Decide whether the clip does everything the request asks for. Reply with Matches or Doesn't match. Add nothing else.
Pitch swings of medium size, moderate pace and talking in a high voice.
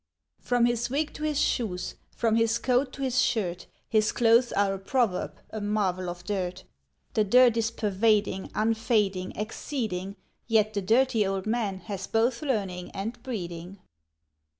Matches